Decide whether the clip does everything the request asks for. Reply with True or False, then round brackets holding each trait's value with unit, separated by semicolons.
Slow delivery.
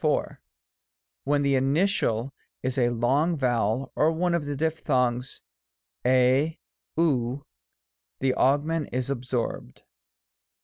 True (115 wpm)